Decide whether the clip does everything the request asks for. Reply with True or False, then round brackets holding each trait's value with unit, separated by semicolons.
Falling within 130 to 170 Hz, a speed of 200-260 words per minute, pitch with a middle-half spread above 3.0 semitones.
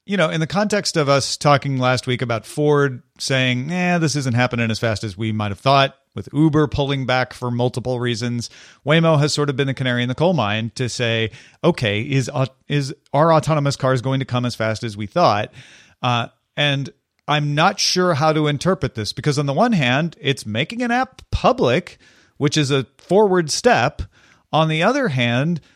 True (140 Hz; 205 wpm; 4.1 semitones)